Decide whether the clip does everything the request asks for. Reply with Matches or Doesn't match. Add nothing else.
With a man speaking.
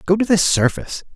Matches